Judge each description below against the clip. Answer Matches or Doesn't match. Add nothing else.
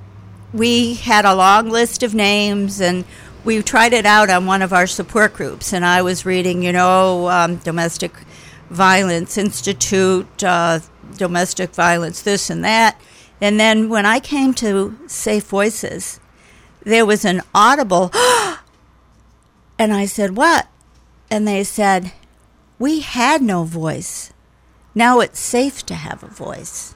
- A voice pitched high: Matches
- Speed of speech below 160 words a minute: Matches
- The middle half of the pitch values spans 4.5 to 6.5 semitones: Doesn't match